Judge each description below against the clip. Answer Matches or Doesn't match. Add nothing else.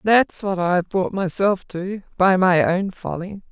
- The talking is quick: Doesn't match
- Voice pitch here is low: Doesn't match